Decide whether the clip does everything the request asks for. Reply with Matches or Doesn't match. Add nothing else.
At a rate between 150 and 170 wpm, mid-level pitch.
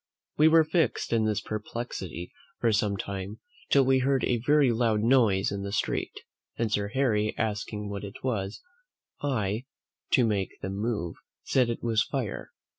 Doesn't match